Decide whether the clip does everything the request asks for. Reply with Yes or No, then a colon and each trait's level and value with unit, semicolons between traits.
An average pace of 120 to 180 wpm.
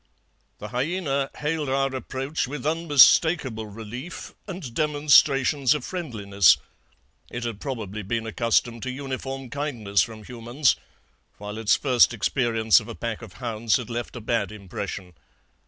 Yes: average, 140 wpm